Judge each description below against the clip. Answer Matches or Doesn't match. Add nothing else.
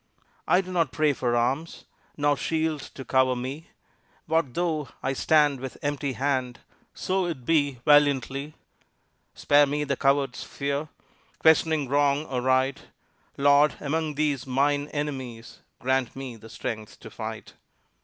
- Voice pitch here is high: Doesn't match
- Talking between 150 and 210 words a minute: Doesn't match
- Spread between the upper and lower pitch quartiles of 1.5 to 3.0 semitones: Matches